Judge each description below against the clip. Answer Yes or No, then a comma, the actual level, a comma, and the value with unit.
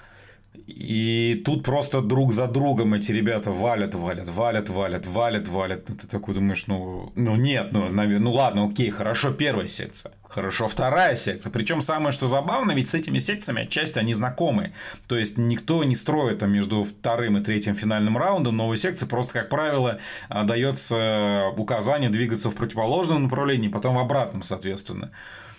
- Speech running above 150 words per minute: Yes, fast, 160 wpm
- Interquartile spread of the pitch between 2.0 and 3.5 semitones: No, average, 4.1 semitones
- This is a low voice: Yes, low, 115 Hz